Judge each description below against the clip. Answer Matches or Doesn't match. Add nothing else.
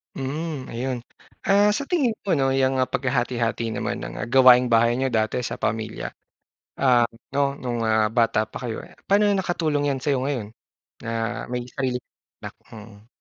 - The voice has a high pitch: Doesn't match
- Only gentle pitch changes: Doesn't match